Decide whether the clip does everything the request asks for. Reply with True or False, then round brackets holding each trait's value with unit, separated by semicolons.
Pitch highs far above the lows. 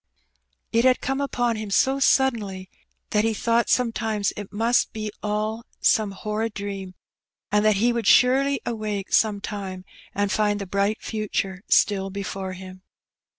False (2.6 semitones)